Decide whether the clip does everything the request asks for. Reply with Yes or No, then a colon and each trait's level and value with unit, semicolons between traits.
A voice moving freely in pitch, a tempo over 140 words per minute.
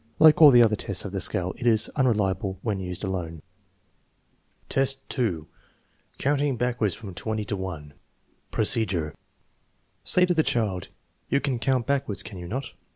Yes: wide, 5.7 semitones; average, 160 wpm